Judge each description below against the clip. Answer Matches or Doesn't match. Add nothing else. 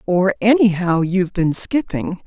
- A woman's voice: Matches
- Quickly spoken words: Doesn't match